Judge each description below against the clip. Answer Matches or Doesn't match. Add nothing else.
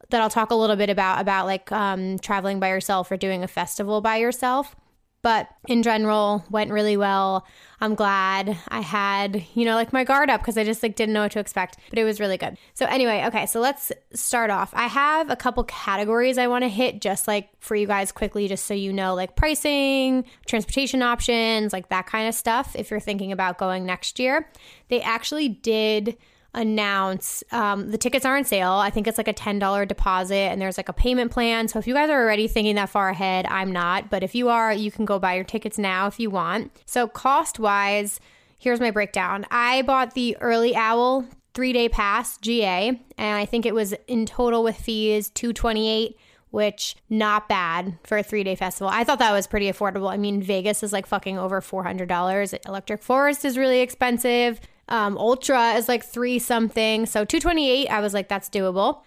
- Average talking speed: Doesn't match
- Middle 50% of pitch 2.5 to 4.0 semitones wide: Matches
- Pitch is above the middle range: Matches